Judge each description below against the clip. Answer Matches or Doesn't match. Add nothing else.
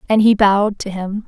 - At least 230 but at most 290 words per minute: Matches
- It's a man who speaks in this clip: Doesn't match